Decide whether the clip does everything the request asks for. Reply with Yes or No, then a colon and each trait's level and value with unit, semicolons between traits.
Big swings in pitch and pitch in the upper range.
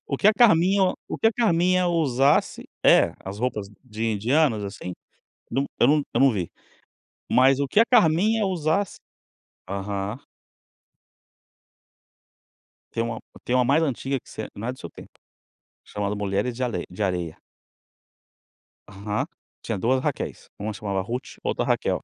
No: wide, 7.6 semitones; low, 125 Hz